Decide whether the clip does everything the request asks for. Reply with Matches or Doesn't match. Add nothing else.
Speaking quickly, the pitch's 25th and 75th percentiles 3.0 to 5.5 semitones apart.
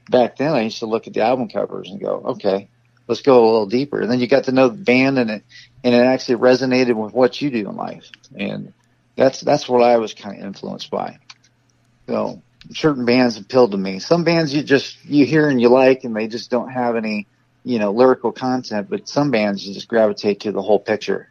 Doesn't match